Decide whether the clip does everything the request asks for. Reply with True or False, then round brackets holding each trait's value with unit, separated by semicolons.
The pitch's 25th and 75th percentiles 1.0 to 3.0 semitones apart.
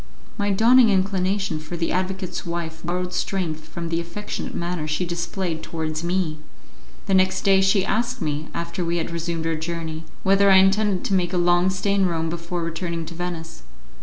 True (2.5 semitones)